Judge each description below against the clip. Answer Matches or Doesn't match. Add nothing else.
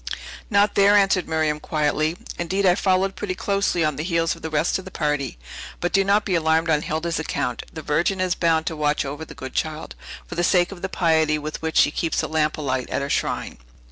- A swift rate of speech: Matches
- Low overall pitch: Doesn't match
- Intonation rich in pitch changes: Doesn't match